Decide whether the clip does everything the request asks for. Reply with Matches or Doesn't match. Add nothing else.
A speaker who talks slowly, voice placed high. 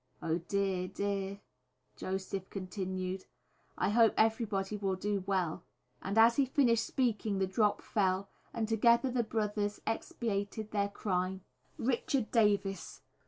Matches